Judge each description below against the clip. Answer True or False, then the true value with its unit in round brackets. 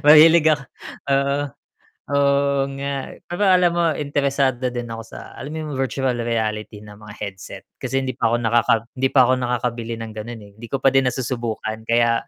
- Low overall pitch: True (130 Hz)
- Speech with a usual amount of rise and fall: True (3.3 semitones)